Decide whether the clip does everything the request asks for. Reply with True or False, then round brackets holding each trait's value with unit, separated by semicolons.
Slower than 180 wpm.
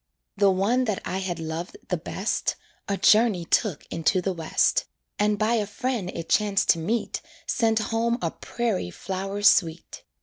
True (165 wpm)